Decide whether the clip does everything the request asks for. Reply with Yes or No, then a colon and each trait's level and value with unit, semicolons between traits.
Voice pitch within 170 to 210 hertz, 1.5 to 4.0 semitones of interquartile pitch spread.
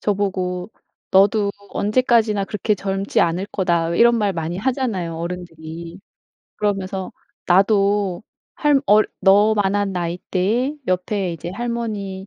Yes: high, 195 Hz; average, 2.8 semitones